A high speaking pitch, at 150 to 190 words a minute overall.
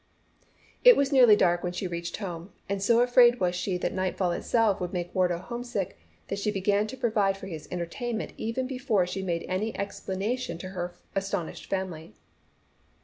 Yes: high, 195 Hz; average, 180 wpm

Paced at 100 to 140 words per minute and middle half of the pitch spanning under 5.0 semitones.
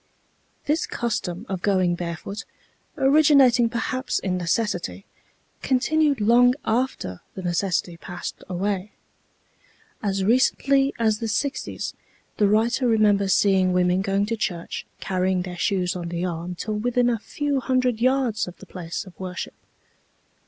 No: slow, 135 wpm; average, 5.3 semitones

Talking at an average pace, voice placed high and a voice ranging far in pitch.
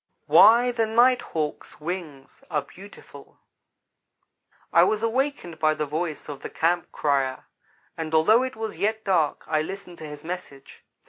No: average, 150 wpm; medium, 175 Hz; wide, 6.2 semitones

